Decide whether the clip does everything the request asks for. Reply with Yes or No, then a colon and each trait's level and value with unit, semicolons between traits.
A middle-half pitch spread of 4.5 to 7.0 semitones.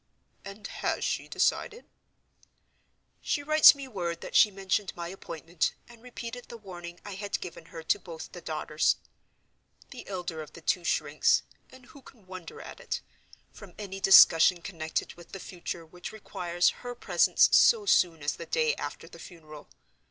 Yes: average, 5.1 semitones